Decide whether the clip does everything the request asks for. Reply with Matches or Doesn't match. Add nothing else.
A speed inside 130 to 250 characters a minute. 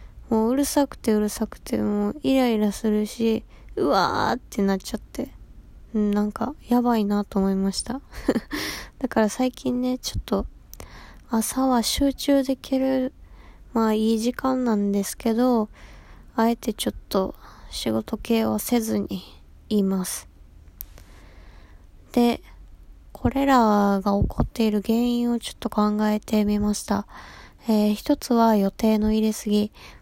Doesn't match